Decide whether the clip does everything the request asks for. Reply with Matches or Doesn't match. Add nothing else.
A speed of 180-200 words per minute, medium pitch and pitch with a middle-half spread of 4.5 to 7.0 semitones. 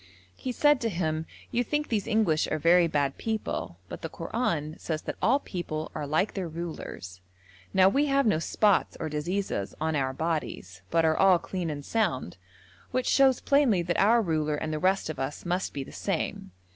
Matches